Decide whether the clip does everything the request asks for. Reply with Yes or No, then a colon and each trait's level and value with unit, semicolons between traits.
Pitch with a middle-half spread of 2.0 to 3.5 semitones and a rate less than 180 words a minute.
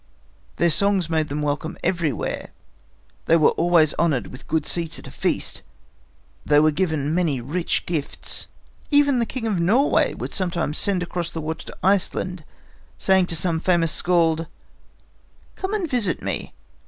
Yes: average, 3.2 semitones; average, 155 wpm